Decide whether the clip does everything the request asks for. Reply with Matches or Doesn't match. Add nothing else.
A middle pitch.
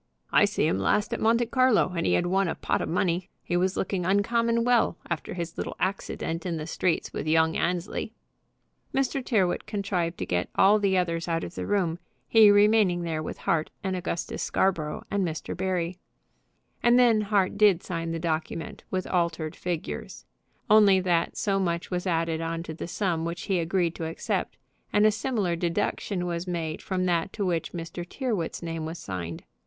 Matches